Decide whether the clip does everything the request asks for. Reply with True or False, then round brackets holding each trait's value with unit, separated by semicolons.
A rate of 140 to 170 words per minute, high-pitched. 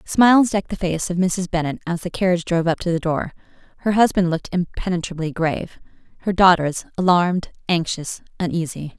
False (165 wpm; 175 Hz)